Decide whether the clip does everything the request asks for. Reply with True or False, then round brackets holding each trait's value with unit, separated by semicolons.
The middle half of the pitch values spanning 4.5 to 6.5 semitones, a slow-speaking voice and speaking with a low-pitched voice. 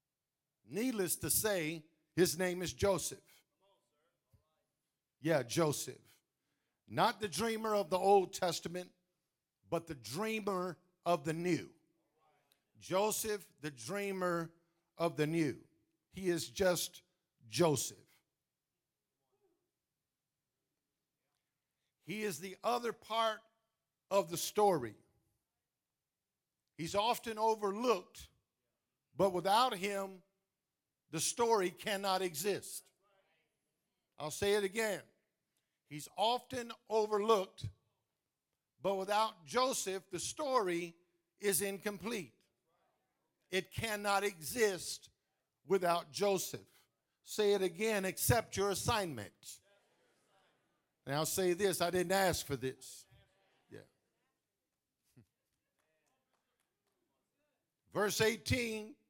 False (5.2 semitones; 85 wpm; 180 Hz)